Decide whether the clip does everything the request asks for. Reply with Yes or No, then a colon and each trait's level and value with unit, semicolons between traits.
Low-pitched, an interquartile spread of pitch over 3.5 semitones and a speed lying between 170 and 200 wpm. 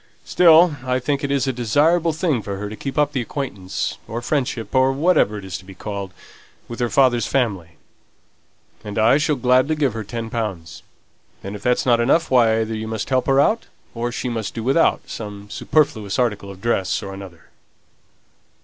Yes: low, 120 Hz; average, 4.9 semitones; average, 190 wpm